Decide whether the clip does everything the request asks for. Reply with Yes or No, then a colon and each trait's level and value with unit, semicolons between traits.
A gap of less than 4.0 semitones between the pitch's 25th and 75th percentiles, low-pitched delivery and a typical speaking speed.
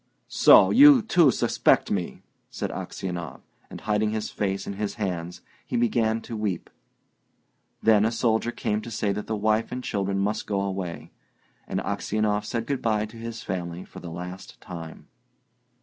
Yes: average, 2.8 semitones; low, 105 Hz; average, 165 wpm